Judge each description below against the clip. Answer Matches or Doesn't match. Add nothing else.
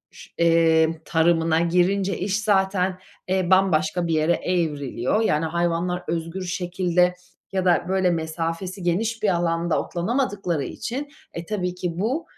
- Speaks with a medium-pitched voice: Matches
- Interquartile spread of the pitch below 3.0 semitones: Matches